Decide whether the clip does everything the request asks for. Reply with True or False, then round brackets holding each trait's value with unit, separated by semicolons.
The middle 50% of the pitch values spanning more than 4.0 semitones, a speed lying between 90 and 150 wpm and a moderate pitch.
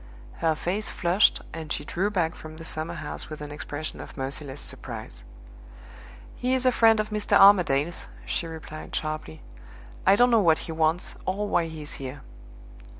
False (4.5 semitones; 170 wpm; 165 Hz)